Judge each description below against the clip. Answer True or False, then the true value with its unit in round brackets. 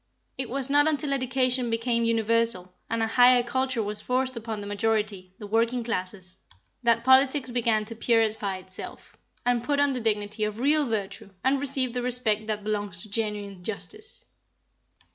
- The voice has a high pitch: True (230 Hz)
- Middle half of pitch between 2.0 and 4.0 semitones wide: True (3.4 semitones)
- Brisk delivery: False (165 wpm)